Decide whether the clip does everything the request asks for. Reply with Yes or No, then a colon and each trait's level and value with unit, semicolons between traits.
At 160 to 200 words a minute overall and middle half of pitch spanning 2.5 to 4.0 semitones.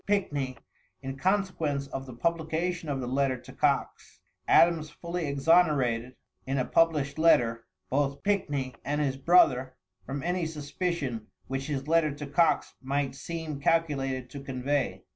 No: average, 145 wpm; average, 3.6 semitones